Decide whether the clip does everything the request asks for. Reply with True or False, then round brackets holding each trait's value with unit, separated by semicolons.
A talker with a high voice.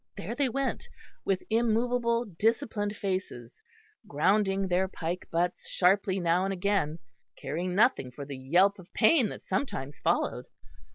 True (195 Hz)